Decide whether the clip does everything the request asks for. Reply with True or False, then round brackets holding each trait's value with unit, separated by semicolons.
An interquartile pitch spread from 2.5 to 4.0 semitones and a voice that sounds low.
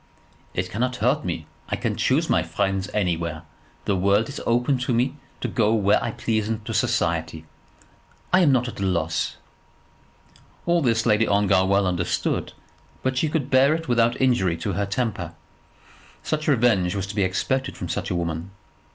False (5.3 semitones; 105 Hz)